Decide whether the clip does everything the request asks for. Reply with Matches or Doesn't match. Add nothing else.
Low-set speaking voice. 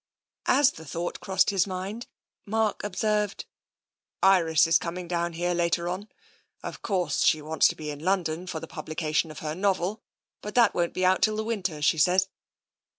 Doesn't match